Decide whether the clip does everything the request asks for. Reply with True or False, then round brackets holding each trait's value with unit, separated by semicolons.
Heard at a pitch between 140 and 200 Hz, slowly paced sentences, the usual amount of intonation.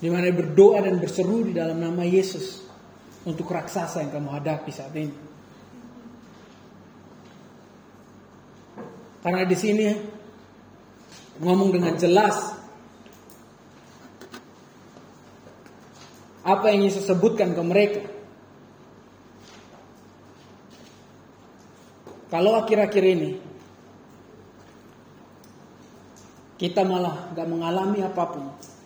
True (185 Hz; 75 wpm; 3.5 semitones)